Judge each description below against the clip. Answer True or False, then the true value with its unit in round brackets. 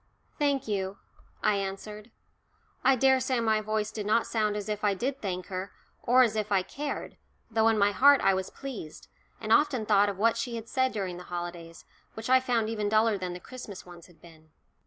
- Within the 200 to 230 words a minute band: True (205 wpm)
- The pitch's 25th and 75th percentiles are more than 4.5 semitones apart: False (3.4 semitones)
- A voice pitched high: True (215 Hz)